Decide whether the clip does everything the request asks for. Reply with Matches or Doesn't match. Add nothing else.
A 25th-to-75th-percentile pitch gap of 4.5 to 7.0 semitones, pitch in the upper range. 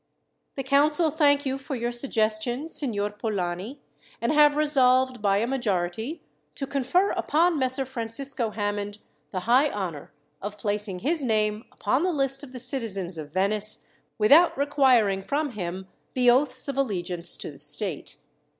Matches